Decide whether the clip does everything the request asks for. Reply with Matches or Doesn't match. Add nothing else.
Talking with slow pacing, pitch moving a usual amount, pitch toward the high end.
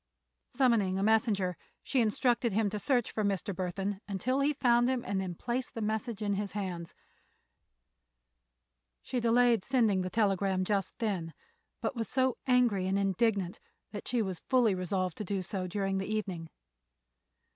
Doesn't match